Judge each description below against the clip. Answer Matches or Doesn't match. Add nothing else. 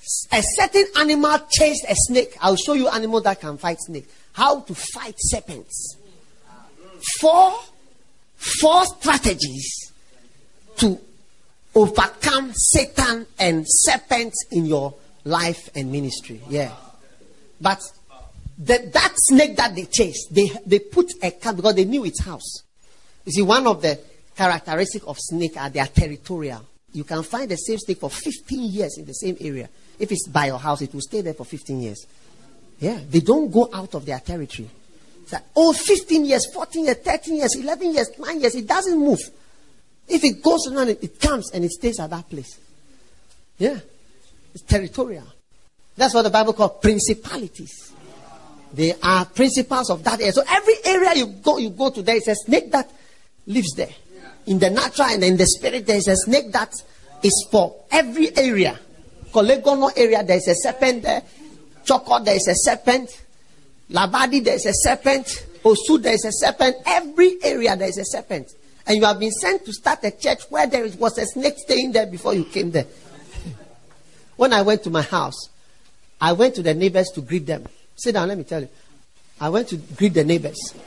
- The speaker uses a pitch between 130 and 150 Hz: Doesn't match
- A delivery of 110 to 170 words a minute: Doesn't match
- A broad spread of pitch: Matches